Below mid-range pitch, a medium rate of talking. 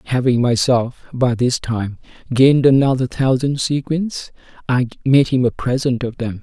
Yes: low, 125 Hz; average, 150 wpm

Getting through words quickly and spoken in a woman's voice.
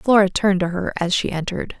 Yes: fast, 235 wpm; female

